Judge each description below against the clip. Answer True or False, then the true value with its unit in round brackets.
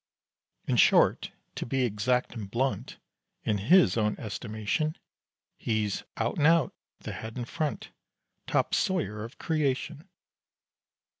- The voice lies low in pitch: True (120 Hz)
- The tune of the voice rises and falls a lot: True (5.7 semitones)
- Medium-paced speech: False (125 wpm)